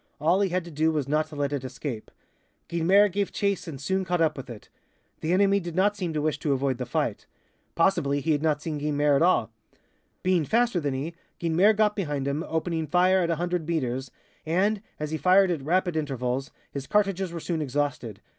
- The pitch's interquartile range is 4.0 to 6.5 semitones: Yes, average, 4.3 semitones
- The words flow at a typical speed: No, fast, 210 wpm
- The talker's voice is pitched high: No, medium, 160 Hz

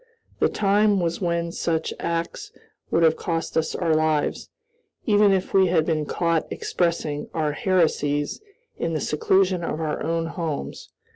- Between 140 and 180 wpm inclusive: Yes, average, 150 wpm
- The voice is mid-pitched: Yes, medium, 165 Hz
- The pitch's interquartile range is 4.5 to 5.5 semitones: No, narrow, 2.5 semitones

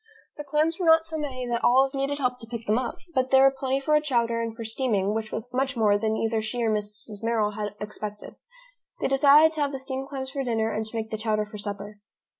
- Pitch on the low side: No, high, 235 Hz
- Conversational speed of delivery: No, fast, 250 wpm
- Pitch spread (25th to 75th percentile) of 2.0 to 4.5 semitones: Yes, average, 3.9 semitones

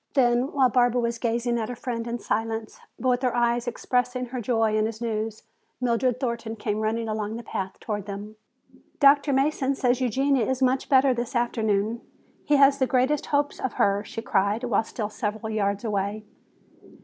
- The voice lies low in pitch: No, high, 235 Hz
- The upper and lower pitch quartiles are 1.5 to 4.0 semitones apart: Yes, average, 2.7 semitones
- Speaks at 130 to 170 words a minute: No, average, 185 wpm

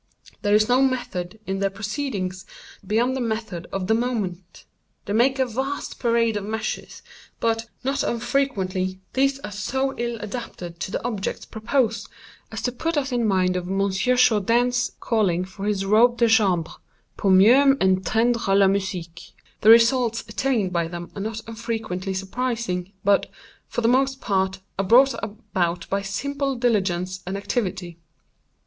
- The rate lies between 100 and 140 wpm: No, average, 155 wpm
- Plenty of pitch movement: No, average, 4.3 semitones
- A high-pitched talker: Yes, high, 215 Hz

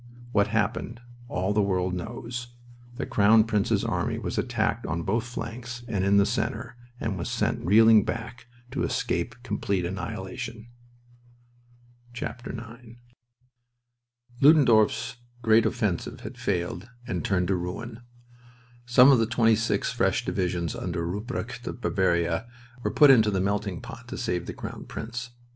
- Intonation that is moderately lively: Yes, average, 3.9 semitones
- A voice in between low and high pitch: No, low, 110 Hz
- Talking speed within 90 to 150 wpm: Yes, average, 145 wpm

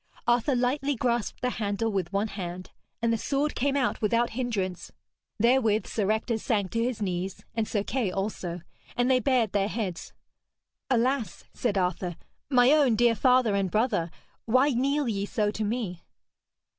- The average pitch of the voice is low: No, high, 225 Hz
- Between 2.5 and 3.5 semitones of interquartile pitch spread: No, average, 3.9 semitones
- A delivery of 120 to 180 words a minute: Yes, average, 165 wpm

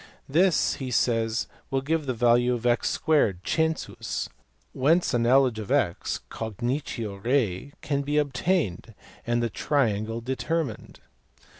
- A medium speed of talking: No, slow, 130 wpm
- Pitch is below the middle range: Yes, low, 125 Hz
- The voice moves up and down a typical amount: Yes, average, 4.0 semitones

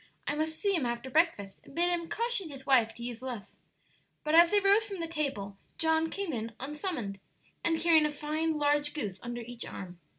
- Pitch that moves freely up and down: Yes, wide, 5.7 semitones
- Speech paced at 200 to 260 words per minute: Yes, fast, 205 wpm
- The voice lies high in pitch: Yes, very high, 300 Hz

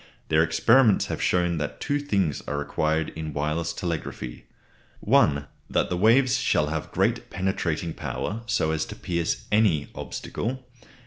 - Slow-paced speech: No, average, 145 wpm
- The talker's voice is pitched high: No, very low, 85 Hz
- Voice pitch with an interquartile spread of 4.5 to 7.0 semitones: Yes, average, 5.1 semitones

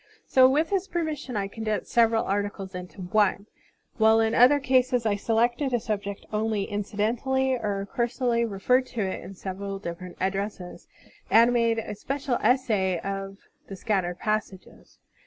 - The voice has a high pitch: Yes, high, 220 Hz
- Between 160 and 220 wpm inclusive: No, average, 150 wpm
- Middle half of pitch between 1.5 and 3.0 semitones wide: No, average, 3.8 semitones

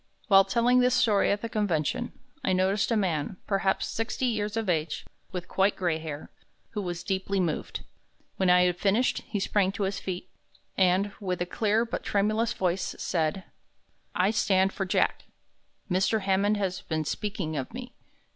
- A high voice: Yes, high, 195 Hz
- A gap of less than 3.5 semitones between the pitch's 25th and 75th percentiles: Yes, average, 2.8 semitones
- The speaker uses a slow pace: No, average, 170 wpm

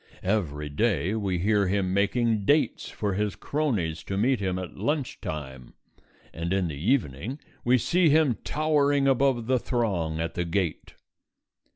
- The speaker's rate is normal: Yes, average, 155 wpm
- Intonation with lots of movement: Yes, wide, 6.8 semitones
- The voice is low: Yes, low, 100 Hz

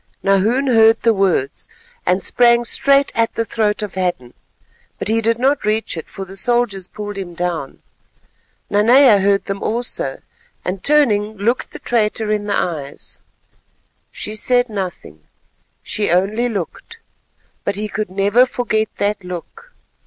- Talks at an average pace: Yes, average, 145 wpm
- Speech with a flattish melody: No, average, 3.5 semitones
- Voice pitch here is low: No, high, 210 Hz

